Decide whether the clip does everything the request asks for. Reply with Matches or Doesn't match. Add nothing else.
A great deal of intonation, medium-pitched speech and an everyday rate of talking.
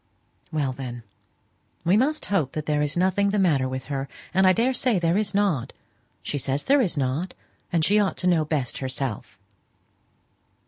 Matches